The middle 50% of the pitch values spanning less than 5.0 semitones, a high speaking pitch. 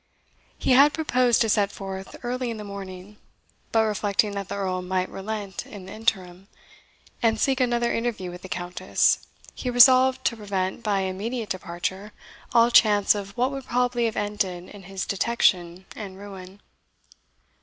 Yes: average, 3.8 semitones; high, 205 Hz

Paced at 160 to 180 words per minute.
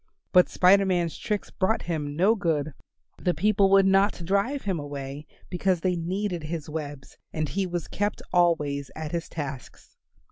Yes: average, 165 wpm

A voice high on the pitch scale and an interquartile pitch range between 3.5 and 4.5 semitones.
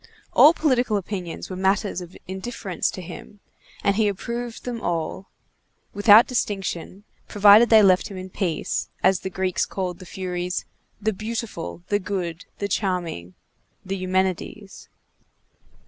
No: high, 195 Hz; narrow, 2.5 semitones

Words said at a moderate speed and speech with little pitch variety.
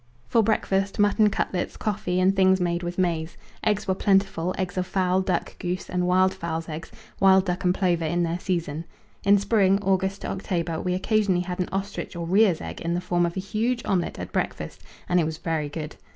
No: fast, 210 wpm; narrow, 2.0 semitones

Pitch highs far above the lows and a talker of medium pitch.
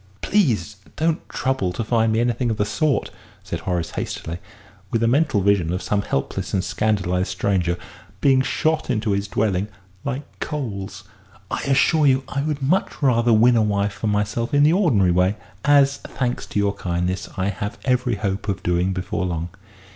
No: wide, 5.8 semitones; low, 105 Hz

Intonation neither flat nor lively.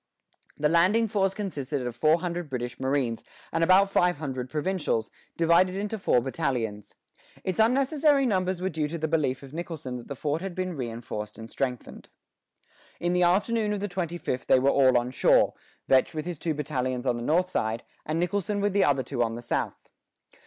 No: wide, 6.3 semitones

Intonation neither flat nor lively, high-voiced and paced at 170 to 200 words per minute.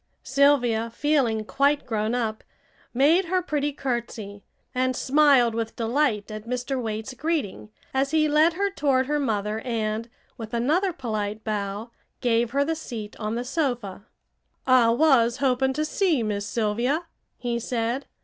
No: average, 4.4 semitones; high, 245 Hz; average, 150 wpm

